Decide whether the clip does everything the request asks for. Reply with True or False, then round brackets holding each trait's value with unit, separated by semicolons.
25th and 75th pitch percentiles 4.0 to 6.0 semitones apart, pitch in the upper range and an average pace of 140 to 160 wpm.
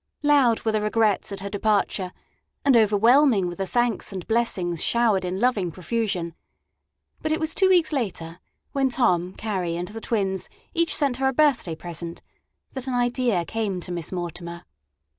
False (5.5 semitones; 215 Hz; 170 wpm)